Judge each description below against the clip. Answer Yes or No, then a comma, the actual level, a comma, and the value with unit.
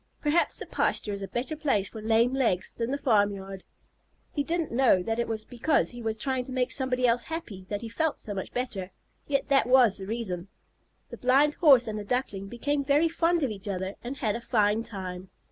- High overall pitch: Yes, high, 235 Hz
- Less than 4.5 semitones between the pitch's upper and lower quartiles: No, average, 4.9 semitones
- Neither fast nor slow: No, fast, 215 wpm